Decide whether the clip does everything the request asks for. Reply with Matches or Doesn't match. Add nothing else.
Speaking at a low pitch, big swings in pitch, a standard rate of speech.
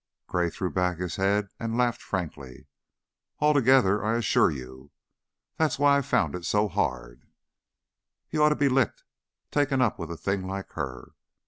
Matches